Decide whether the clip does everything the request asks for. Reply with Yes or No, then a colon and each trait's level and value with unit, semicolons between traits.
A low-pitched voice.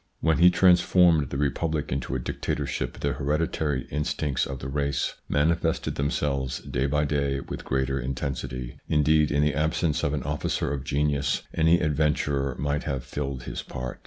Yes: very low, 70 Hz